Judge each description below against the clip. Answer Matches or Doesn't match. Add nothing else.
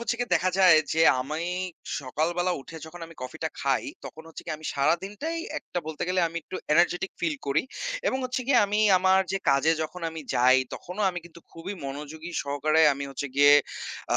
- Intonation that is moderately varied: Matches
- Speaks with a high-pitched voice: Doesn't match